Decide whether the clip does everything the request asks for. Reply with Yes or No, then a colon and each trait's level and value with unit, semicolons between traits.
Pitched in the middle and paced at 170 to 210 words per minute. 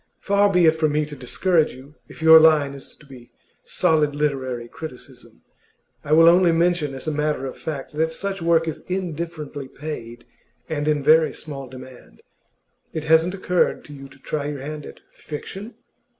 Yes: medium, 155 Hz; average, 180 wpm